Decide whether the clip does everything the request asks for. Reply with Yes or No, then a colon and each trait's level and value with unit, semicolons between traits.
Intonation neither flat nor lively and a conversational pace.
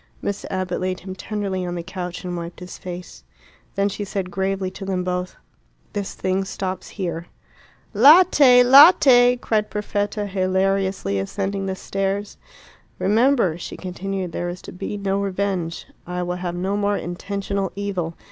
No: narrow, 1.9 semitones; average, 155 wpm